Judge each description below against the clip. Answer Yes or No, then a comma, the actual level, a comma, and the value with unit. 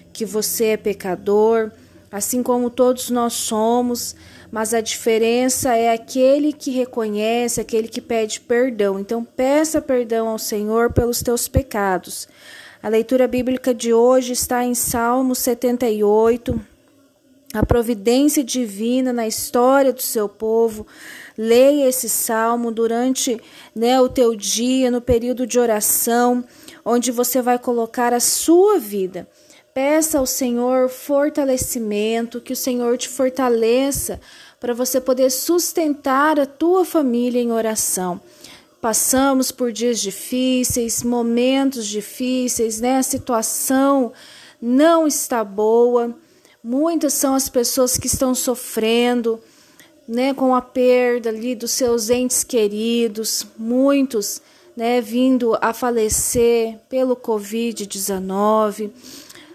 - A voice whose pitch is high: Yes, high, 245 Hz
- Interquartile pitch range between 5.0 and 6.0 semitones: No, narrow, 2.4 semitones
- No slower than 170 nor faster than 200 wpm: No, slow, 120 wpm